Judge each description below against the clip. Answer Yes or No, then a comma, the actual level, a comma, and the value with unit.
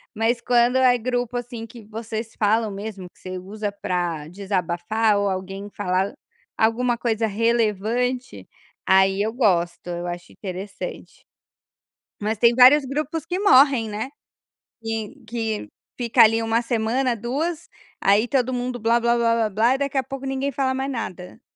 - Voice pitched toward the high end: Yes, high, 225 Hz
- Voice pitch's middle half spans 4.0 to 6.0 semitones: No, average, 3.6 semitones